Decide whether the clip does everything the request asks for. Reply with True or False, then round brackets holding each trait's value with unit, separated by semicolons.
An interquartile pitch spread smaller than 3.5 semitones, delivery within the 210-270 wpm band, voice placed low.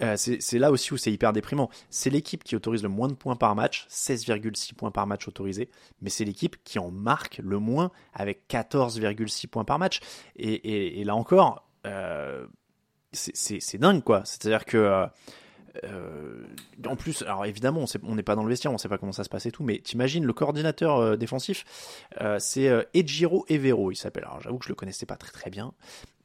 False (4.3 semitones; 215 wpm; 115 Hz)